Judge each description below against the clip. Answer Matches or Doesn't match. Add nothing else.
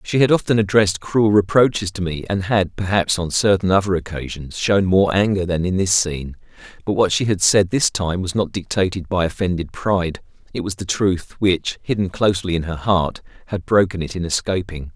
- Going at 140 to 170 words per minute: Doesn't match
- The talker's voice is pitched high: Doesn't match